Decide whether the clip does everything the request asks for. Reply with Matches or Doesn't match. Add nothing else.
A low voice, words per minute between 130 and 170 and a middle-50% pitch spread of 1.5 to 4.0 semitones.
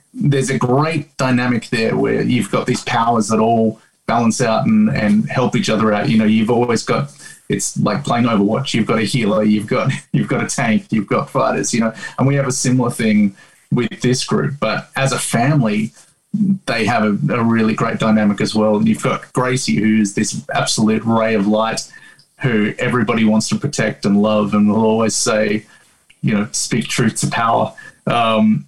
Doesn't match